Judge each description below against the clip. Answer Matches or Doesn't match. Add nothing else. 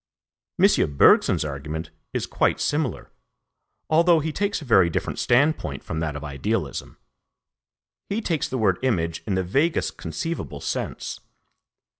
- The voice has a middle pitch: Doesn't match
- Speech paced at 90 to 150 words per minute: Matches